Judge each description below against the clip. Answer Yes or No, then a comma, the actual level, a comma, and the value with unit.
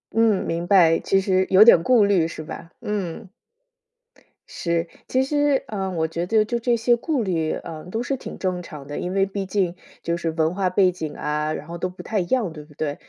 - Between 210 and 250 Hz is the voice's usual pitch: No, medium, 185 Hz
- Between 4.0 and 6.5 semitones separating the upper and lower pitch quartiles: Yes, average, 4.3 semitones